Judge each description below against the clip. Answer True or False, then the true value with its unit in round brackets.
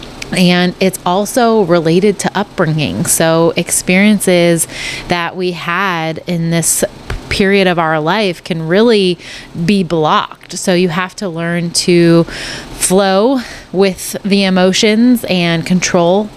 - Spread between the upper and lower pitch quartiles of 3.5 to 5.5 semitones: False (2.6 semitones)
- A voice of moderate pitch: True (180 Hz)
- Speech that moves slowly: True (120 wpm)